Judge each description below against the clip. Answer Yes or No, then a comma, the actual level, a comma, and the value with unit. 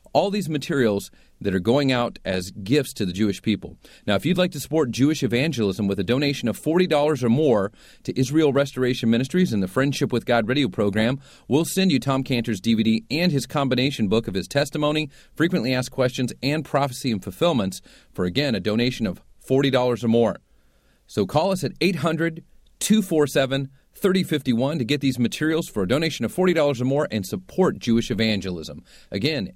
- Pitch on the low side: Yes, low, 130 Hz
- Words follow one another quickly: No, average, 185 wpm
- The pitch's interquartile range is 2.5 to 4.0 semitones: No, average, 4.9 semitones